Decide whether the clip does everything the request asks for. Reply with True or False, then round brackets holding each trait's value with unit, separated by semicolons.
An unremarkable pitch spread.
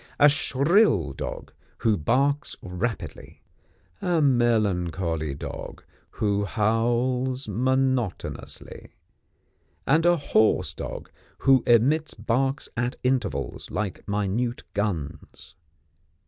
True (4.8 semitones)